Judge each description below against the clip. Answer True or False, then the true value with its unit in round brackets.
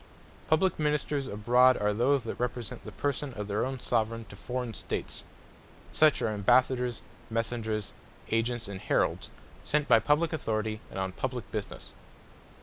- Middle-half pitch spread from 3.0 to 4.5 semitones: True (3.6 semitones)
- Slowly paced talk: False (145 wpm)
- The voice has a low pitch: True (120 Hz)